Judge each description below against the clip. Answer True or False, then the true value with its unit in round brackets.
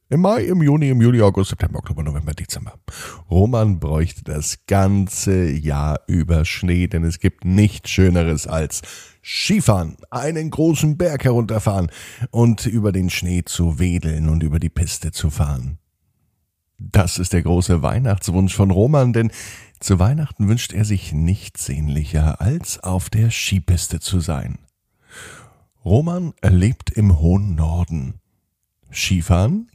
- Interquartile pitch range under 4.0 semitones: False (4.7 semitones)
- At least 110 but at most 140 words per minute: True (135 wpm)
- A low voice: True (95 Hz)